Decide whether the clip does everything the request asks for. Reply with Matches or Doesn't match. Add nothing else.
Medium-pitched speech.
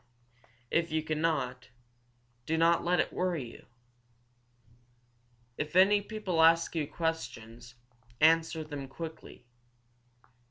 Matches